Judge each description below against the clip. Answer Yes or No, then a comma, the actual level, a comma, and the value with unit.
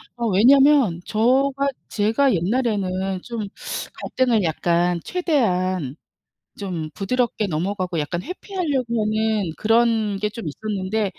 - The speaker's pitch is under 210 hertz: No, high, 215 Hz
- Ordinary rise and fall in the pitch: Yes, average, 5.0 semitones